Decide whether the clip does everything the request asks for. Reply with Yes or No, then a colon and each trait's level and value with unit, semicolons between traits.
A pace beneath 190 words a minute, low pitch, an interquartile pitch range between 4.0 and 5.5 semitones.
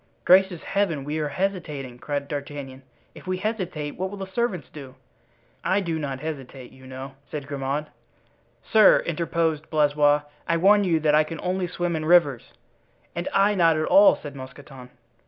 No: average, 170 wpm; medium, 155 Hz; average, 4.4 semitones